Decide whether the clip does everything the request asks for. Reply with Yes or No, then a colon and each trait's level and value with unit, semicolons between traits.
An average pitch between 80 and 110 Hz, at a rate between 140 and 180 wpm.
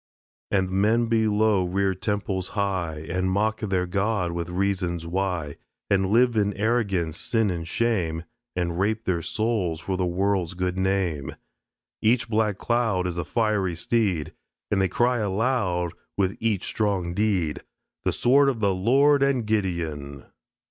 Yes: very low, 95 Hz; average, 150 wpm